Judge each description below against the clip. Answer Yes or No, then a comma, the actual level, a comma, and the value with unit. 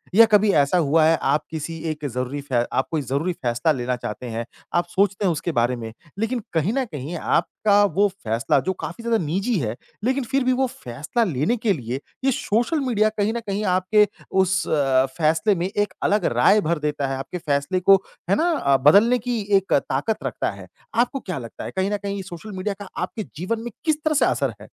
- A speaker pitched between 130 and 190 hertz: Yes, medium, 185 Hz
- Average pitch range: No, wide, 7.1 semitones